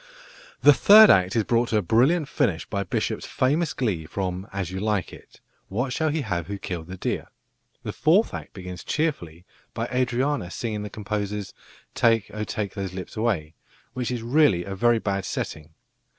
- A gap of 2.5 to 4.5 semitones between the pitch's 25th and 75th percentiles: No, average, 5.1 semitones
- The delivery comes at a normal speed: Yes, average, 180 wpm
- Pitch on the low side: Yes, low, 105 Hz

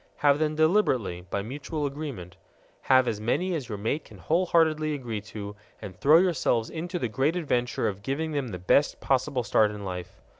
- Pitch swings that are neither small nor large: No, wide, 6.7 semitones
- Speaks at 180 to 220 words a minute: Yes, average, 185 wpm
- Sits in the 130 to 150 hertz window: Yes, low, 135 Hz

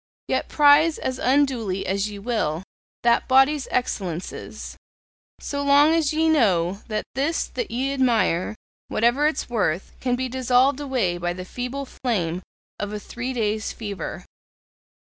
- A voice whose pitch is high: Yes, high, 245 Hz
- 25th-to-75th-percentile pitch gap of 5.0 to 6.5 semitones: Yes, wide, 5.6 semitones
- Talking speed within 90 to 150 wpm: Yes, average, 145 wpm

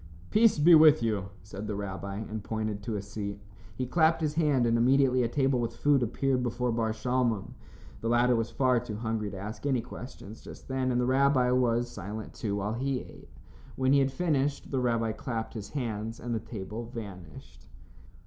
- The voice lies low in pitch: Yes, low, 120 Hz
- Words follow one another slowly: No, average, 195 wpm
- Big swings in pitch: No, average, 3.3 semitones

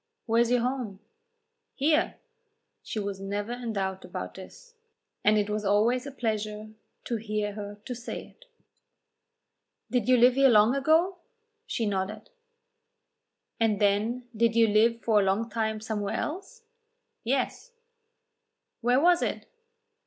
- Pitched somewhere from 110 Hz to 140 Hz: No, high, 225 Hz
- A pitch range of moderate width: Yes, average, 3.1 semitones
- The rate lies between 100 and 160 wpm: Yes, average, 140 wpm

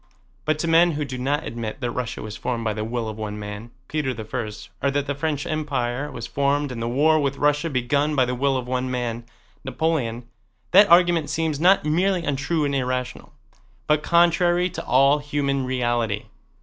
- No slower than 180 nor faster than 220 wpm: Yes, average, 190 wpm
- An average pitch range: Yes, average, 4.0 semitones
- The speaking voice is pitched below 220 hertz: Yes, medium, 140 Hz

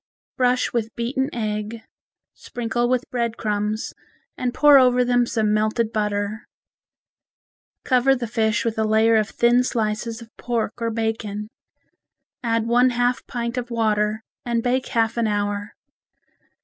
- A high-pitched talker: Yes, high, 230 Hz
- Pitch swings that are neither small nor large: No, narrow, 2.1 semitones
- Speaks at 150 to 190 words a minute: No, average, 140 wpm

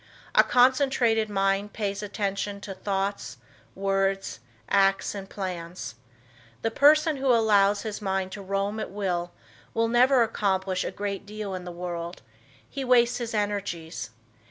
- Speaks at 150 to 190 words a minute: No, average, 140 wpm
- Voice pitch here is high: Yes, high, 200 Hz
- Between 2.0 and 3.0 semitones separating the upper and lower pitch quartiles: Yes, narrow, 2.6 semitones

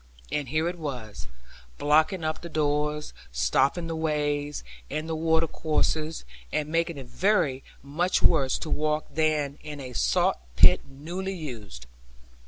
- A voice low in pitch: No, medium, 150 Hz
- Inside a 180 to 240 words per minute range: No, average, 145 wpm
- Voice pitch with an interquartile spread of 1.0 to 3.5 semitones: Yes, narrow, 2.5 semitones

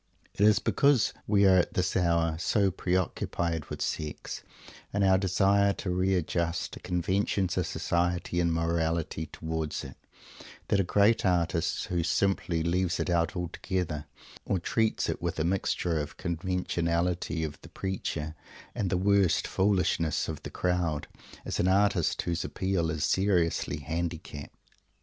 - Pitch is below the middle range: Yes, very low, 90 Hz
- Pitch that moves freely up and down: No, narrow, 2.5 semitones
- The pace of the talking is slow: No, average, 150 wpm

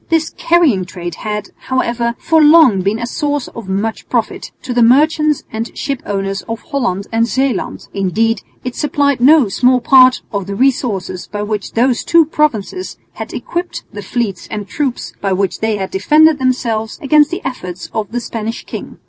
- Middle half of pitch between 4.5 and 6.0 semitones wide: Yes, wide, 5.6 semitones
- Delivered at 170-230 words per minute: Yes, average, 175 wpm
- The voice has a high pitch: Yes, high, 235 Hz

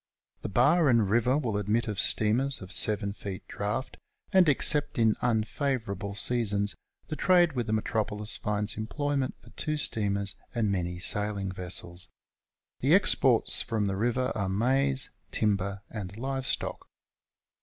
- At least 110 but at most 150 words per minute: Yes, average, 145 wpm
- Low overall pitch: Yes, low, 110 Hz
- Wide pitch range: No, average, 4.3 semitones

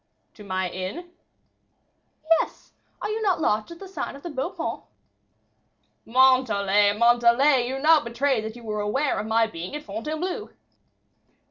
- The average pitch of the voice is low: No, high, 240 Hz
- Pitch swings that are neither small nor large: No, wide, 6.1 semitones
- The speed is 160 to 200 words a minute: No, average, 150 wpm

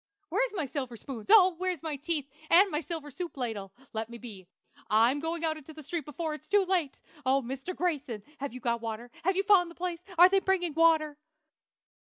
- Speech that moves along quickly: Yes, fast, 210 wpm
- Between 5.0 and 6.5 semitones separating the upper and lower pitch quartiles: Yes, wide, 5.6 semitones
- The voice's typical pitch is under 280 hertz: No, very high, 310 Hz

